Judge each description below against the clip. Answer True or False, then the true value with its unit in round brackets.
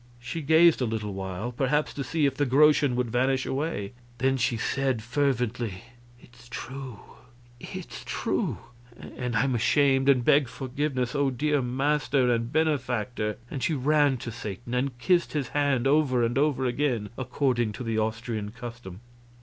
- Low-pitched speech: True (125 Hz)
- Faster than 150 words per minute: True (160 wpm)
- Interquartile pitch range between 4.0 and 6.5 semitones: False (3.1 semitones)